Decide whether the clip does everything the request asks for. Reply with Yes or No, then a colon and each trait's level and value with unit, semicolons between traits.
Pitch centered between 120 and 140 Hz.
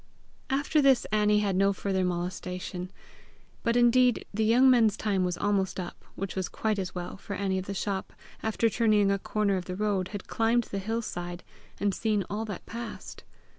No: high, 200 Hz